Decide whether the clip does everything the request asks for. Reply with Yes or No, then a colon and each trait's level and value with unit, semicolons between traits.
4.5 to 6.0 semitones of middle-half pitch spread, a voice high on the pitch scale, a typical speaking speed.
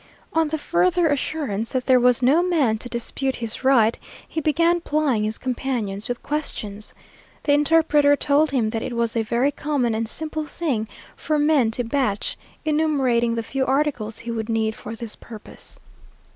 Yes: average, 4.8 semitones; very high, 260 Hz; average, 170 wpm